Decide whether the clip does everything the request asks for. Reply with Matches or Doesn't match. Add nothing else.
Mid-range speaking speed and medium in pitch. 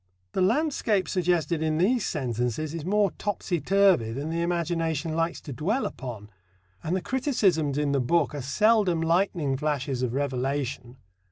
Matches